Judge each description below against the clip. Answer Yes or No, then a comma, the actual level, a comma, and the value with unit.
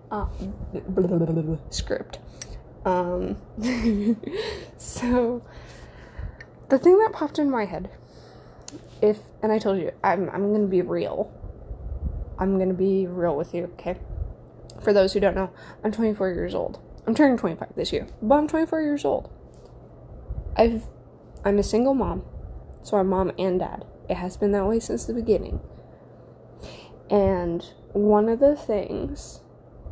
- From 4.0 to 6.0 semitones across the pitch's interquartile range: Yes, average, 4.3 semitones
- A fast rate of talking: No, average, 150 wpm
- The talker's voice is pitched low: No, high, 205 Hz